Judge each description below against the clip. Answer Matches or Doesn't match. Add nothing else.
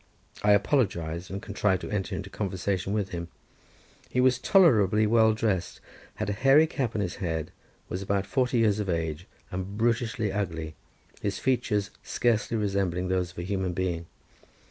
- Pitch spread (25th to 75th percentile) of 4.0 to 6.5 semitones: Doesn't match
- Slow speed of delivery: Doesn't match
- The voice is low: Matches